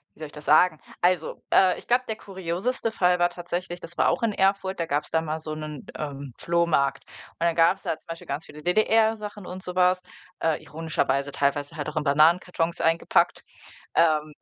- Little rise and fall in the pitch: No, average, 3.2 semitones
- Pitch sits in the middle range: Yes, medium, 170 Hz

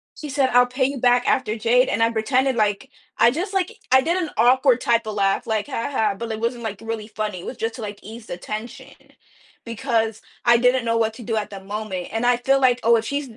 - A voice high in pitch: Yes, high, 230 Hz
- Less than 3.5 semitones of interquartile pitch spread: Yes, average, 2.9 semitones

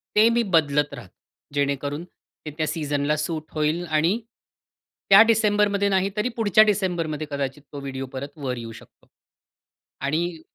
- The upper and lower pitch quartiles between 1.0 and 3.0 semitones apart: No, wide, 5.5 semitones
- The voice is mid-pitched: Yes, medium, 155 Hz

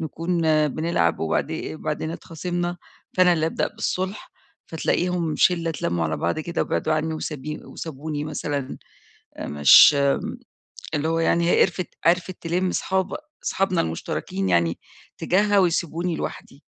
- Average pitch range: Yes, average, 3.1 semitones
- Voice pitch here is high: No, medium, 160 Hz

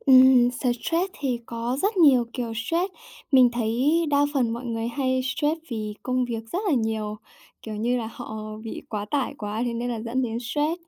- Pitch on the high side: Yes, high, 245 Hz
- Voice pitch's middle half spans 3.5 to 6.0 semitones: No, average, 3.0 semitones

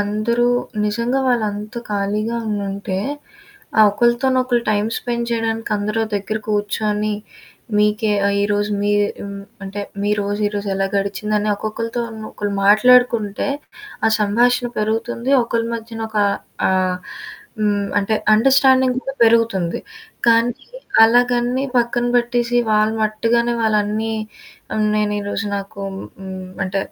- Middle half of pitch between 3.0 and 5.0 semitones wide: No, narrow, 2.4 semitones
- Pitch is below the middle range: No, high, 215 Hz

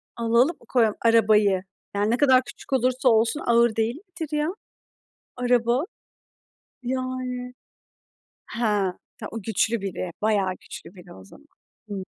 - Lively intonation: No, average, 3.2 semitones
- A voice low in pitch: No, high, 235 Hz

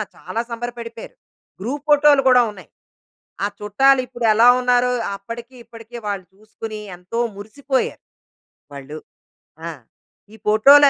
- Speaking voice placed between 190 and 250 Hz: Yes, high, 230 Hz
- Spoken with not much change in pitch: No, average, 3.4 semitones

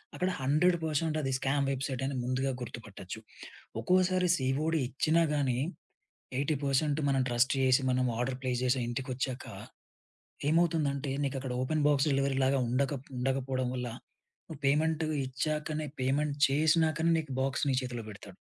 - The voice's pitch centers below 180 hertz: Yes, low, 135 Hz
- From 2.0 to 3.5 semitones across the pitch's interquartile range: Yes, average, 3.0 semitones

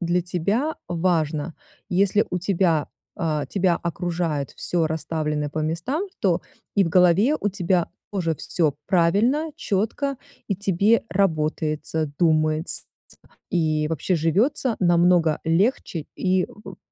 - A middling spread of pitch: Yes, average, 3.7 semitones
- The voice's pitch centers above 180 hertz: No, medium, 175 Hz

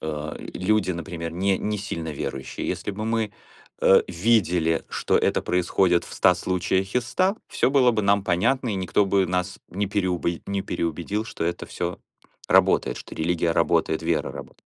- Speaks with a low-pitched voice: Yes, very low, 95 Hz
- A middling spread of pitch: Yes, average, 3.2 semitones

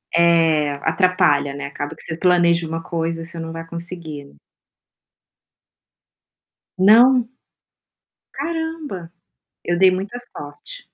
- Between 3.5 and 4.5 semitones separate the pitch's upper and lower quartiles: No, average, 3.0 semitones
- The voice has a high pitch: No, medium, 170 Hz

